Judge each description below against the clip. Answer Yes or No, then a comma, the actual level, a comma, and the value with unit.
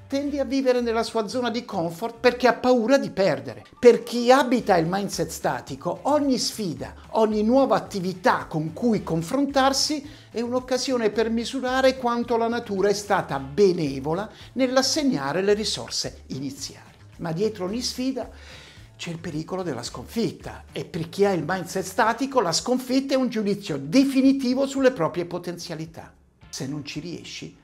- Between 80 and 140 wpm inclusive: No, average, 150 wpm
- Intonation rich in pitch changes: Yes, wide, 7.1 semitones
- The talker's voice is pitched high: Yes, high, 215 Hz